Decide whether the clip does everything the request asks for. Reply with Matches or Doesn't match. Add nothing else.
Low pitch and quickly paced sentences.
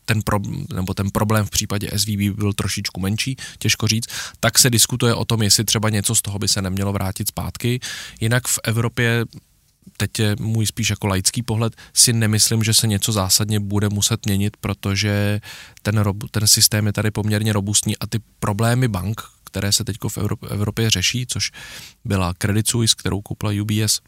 Matches